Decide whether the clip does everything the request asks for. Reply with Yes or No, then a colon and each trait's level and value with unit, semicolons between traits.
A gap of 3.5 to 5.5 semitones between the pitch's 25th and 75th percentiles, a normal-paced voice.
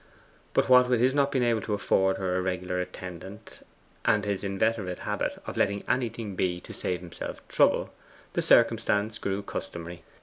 Yes: average, 3.8 semitones; average, 170 wpm